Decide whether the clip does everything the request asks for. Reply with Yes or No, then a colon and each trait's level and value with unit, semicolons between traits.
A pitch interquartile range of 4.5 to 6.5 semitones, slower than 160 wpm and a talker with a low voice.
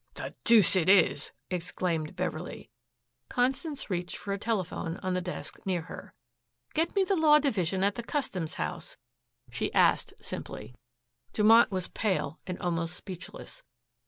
No: average, 4.9 semitones; average, 145 wpm; high, 190 Hz